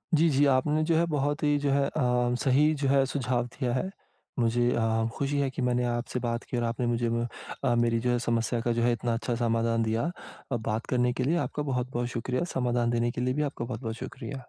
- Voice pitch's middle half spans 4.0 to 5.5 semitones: No, narrow, 2.5 semitones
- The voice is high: No, low, 125 Hz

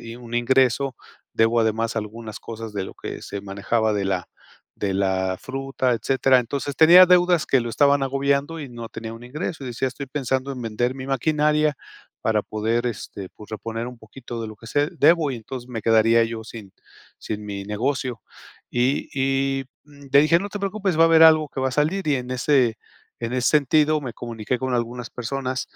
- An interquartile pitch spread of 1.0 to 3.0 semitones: No, average, 3.8 semitones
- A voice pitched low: Yes, low, 125 Hz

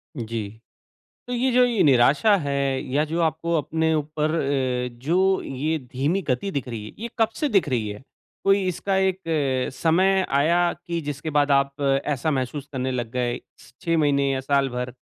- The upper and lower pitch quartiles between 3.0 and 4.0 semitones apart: No, average, 4.7 semitones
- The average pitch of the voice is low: No, medium, 145 Hz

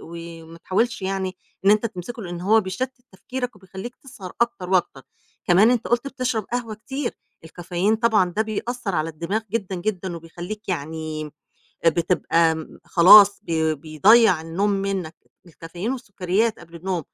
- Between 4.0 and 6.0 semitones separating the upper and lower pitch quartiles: Yes, average, 4.6 semitones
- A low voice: No, high, 190 Hz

